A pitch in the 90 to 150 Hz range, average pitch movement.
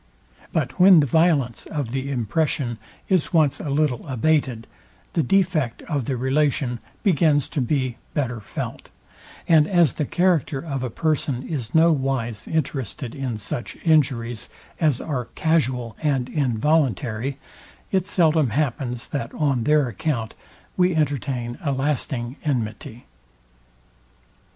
Yes: medium, 140 Hz; average, 4.2 semitones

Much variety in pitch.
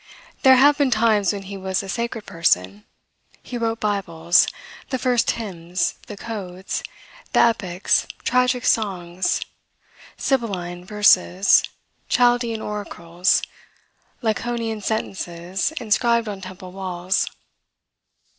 No: average, 4.3 semitones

